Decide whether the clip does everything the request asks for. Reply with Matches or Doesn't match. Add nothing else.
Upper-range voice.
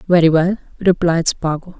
Doesn't match